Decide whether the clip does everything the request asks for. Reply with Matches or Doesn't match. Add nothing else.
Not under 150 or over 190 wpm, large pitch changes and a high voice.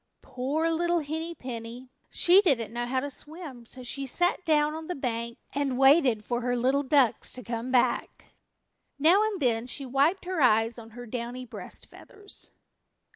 Doesn't match